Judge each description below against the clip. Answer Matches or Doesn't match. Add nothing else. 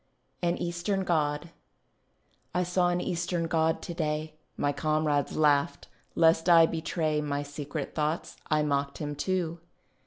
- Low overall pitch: Doesn't match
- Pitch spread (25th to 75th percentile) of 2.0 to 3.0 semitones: Matches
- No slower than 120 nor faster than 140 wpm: Matches